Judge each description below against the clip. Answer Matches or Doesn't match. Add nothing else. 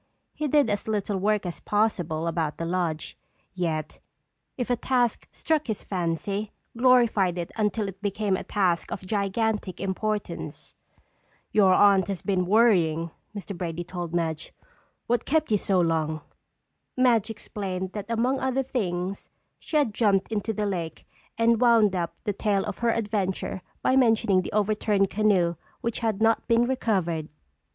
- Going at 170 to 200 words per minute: Doesn't match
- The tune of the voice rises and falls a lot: Doesn't match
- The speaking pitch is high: Matches